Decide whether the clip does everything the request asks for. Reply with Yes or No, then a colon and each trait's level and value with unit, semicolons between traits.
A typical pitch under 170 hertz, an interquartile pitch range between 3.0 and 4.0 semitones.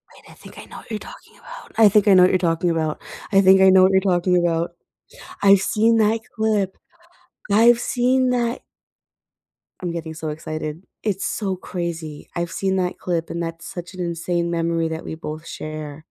No: medium, 180 Hz; average, 3.3 semitones